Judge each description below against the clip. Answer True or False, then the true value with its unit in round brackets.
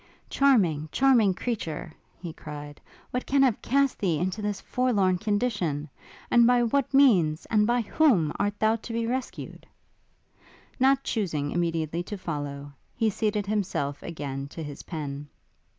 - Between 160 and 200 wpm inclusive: False (145 wpm)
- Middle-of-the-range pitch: False (200 Hz)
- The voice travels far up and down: True (7.4 semitones)